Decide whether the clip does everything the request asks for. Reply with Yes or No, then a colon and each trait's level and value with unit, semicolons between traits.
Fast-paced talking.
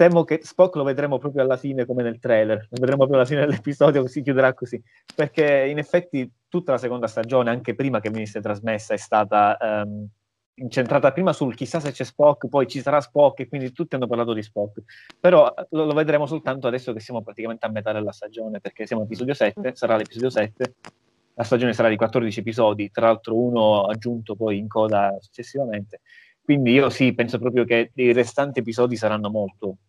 Yes: fast, 200 wpm